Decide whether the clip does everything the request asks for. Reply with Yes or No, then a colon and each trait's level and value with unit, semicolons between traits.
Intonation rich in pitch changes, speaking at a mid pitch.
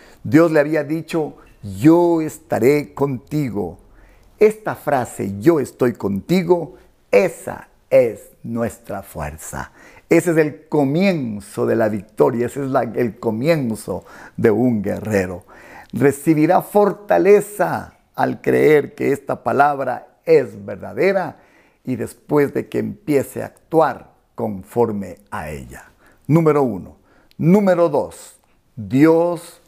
Yes: wide, 7.9 semitones; medium, 145 Hz